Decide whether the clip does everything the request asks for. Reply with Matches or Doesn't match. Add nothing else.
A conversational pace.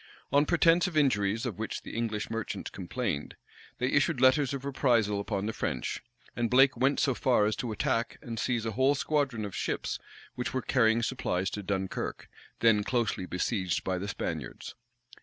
Matches